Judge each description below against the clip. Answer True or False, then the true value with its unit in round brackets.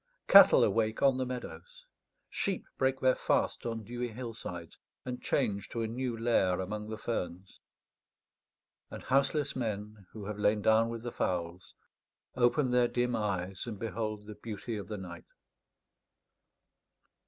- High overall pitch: False (110 Hz)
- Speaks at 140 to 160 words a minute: True (145 wpm)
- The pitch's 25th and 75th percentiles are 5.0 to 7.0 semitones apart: False (3.2 semitones)